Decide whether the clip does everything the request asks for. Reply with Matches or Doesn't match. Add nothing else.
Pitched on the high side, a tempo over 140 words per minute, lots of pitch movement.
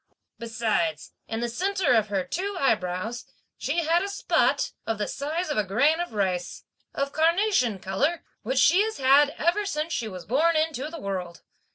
Matches